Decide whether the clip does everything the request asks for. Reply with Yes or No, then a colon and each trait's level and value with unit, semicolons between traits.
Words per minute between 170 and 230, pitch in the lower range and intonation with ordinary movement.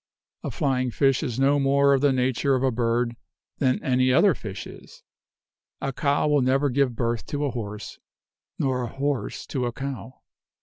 No: average, 180 wpm; low, 130 Hz; narrow, 2.1 semitones